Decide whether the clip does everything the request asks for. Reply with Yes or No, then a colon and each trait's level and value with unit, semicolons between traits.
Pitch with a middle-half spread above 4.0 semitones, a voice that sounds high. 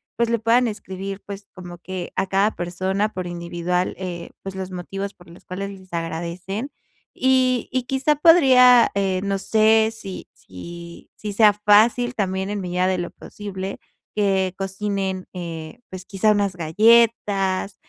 No: average, 2.8 semitones; high, 195 Hz